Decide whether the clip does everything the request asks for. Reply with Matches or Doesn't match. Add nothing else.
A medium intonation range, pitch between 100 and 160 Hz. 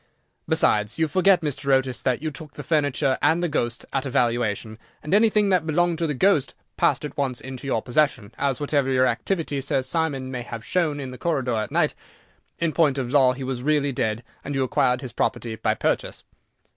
Matches